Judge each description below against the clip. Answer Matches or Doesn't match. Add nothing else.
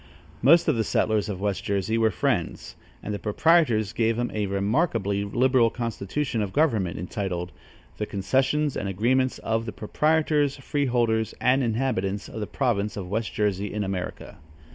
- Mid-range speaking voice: Doesn't match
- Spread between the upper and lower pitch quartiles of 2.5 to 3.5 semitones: Doesn't match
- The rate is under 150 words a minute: Doesn't match